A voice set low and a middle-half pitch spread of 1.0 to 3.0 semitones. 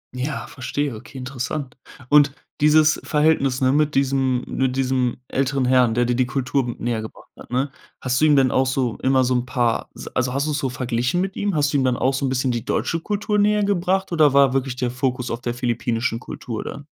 Yes: low, 130 Hz; average, 2.7 semitones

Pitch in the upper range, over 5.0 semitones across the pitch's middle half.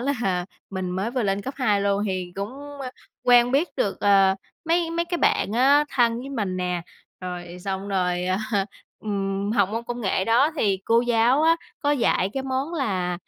Yes: high, 215 Hz; wide, 5.5 semitones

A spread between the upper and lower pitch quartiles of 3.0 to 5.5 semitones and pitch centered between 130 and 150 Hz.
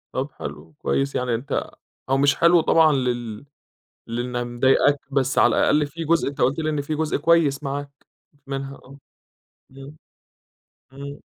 No: narrow, 2.6 semitones; medium, 140 Hz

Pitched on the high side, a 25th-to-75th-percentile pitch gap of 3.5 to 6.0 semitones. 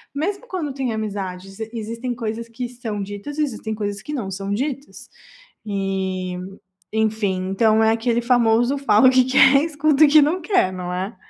Yes: high, 225 Hz; average, 5.2 semitones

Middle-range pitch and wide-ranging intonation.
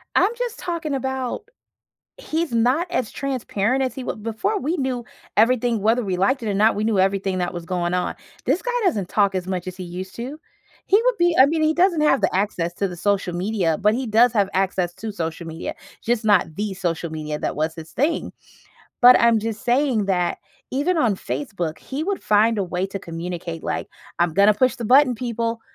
No: high, 220 Hz; wide, 6.1 semitones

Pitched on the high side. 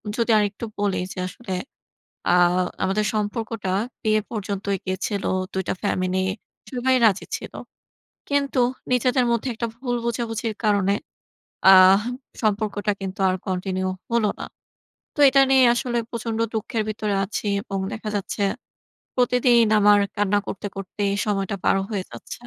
Yes: high, 210 Hz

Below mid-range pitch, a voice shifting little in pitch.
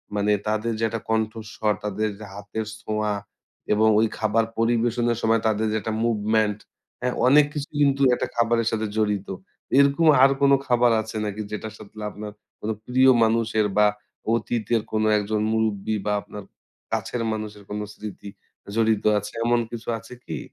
Yes: low, 110 Hz; narrow, 1.7 semitones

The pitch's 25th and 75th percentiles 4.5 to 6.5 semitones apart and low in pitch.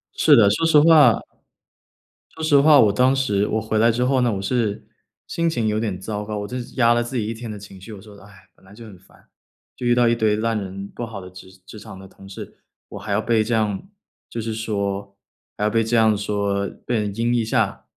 No: average, 2.8 semitones; low, 110 Hz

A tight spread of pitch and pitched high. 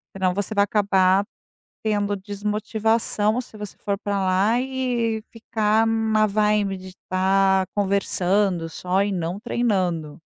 Yes: narrow, 2.3 semitones; high, 205 Hz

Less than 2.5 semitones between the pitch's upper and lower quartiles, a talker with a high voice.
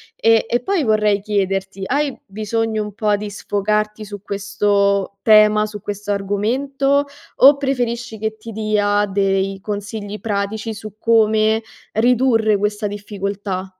Yes: narrow, 1.8 semitones; high, 210 Hz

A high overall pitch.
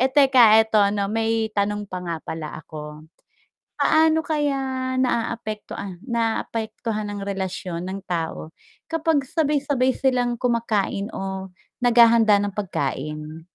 Yes: high, 220 Hz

